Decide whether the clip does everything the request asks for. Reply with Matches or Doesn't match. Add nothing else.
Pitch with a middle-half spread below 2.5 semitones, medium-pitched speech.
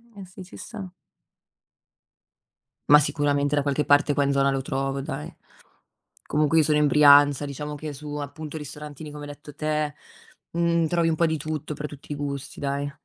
Matches